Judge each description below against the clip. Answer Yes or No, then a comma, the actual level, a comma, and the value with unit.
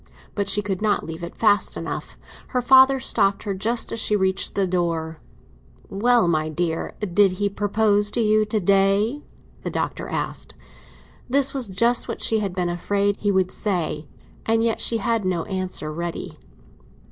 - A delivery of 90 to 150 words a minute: No, average, 170 wpm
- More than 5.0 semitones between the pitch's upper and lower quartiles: No, average, 3.3 semitones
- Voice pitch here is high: Yes, high, 200 Hz